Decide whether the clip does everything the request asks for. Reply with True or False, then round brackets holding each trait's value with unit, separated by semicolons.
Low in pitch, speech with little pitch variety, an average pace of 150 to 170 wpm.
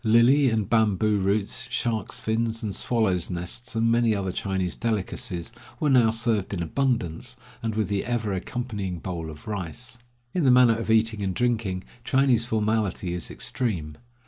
False (110 Hz; 3.7 semitones; 160 wpm)